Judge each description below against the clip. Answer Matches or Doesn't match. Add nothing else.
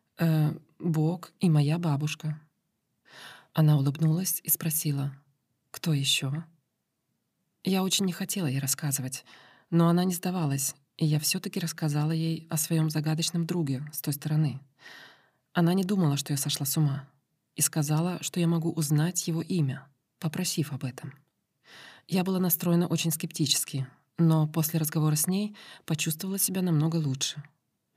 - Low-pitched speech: Doesn't match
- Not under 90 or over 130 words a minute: Doesn't match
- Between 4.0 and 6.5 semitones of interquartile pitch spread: Doesn't match